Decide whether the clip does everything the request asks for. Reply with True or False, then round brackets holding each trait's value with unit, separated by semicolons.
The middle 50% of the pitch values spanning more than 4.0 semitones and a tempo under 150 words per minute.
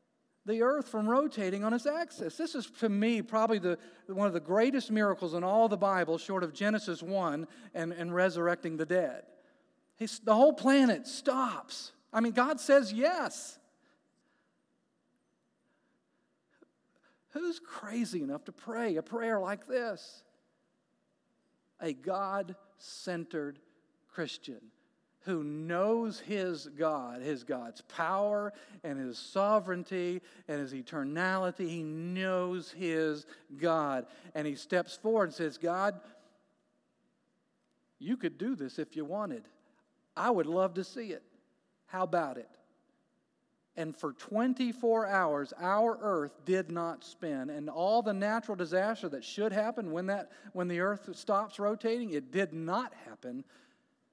True (5.5 semitones; 135 wpm)